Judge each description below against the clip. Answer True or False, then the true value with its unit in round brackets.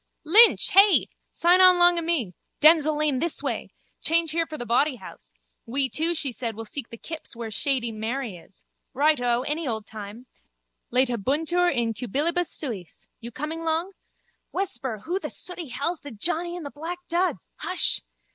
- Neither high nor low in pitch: False (290 Hz)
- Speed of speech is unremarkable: True (165 wpm)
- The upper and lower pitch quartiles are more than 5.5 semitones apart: True (6.1 semitones)